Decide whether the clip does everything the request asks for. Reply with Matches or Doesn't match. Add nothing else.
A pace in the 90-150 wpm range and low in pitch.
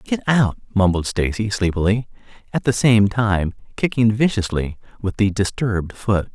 Matches